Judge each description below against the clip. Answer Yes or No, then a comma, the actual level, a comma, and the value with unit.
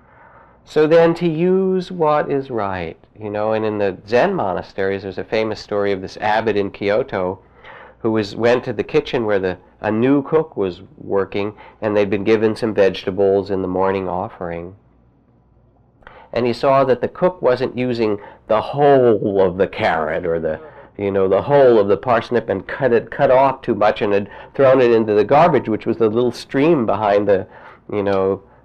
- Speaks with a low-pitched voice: Yes, low, 110 Hz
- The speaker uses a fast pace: No, average, 190 wpm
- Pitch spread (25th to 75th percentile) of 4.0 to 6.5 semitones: Yes, average, 4.4 semitones